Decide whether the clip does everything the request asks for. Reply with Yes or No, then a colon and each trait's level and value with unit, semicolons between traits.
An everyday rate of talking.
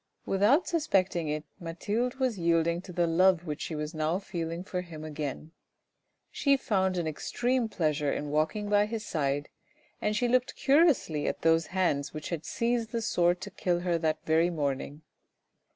Yes: average, 170 wpm